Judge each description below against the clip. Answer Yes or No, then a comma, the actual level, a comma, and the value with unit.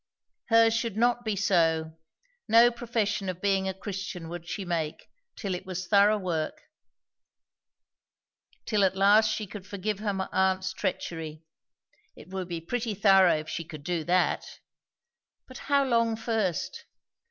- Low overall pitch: No, high, 195 Hz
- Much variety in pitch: No, average, 3.7 semitones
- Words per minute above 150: No, average, 145 wpm